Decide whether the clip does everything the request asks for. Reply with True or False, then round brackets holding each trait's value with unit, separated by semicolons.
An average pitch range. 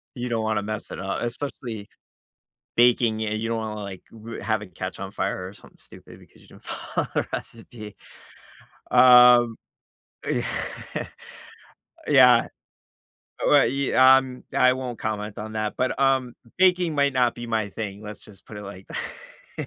True (3.2 semitones)